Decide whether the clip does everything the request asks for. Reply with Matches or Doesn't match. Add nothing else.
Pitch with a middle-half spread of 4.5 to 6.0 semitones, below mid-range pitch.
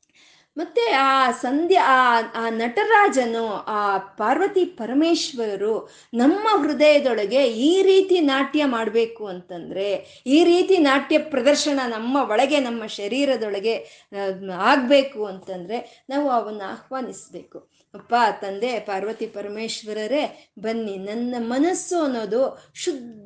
Doesn't match